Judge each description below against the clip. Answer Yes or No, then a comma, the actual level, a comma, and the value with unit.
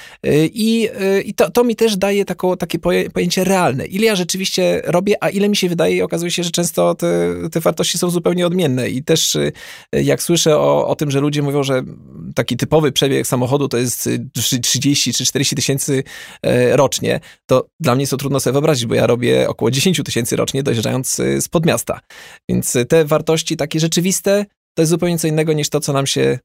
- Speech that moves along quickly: Yes, fast, 195 wpm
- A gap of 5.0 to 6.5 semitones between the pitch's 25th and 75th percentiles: Yes, wide, 5.4 semitones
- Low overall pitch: No, medium, 150 Hz